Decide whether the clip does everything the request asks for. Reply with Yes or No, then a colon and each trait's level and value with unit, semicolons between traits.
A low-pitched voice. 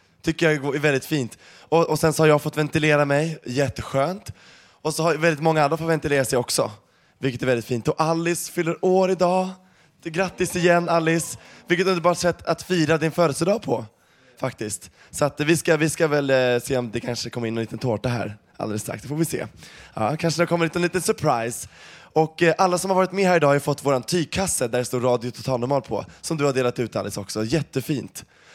No: medium, 150 Hz